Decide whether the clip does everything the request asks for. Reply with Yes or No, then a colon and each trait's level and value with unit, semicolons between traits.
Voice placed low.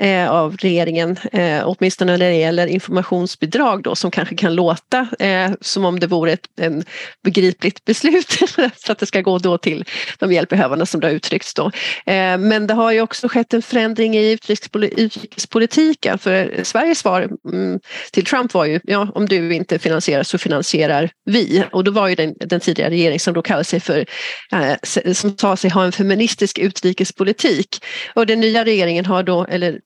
No: high, 190 Hz